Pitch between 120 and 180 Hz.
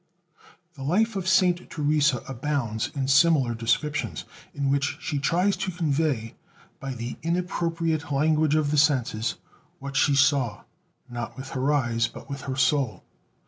Yes: medium, 140 Hz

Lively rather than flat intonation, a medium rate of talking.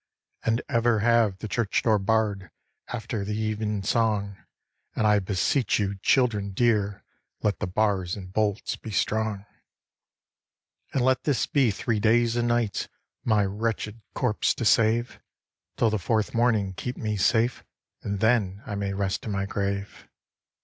No: narrow, 2.5 semitones; average, 150 wpm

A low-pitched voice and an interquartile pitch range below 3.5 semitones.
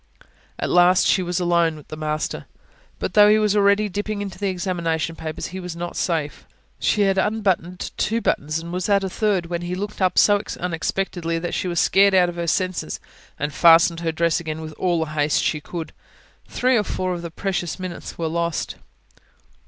No: medium, 175 Hz; average, 2.8 semitones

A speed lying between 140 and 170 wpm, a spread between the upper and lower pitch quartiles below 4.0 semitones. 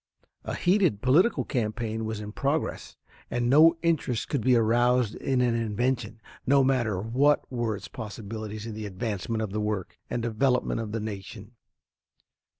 Yes: average, 155 wpm; average, 3.1 semitones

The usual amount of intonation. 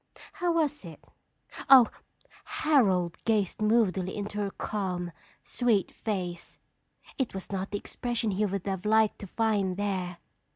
Yes: average, 3.4 semitones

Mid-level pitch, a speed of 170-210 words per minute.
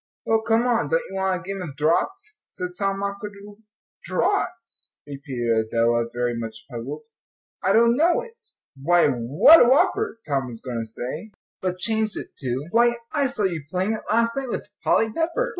No: high, 195 Hz; average, 180 wpm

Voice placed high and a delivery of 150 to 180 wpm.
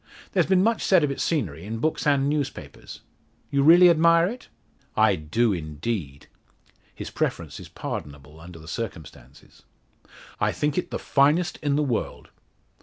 No: low, 135 Hz; average, 155 wpm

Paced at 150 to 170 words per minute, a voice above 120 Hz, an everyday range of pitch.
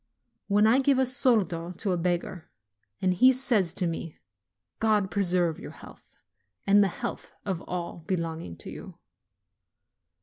Yes: average, 155 wpm; medium, 185 Hz; average, 4.1 semitones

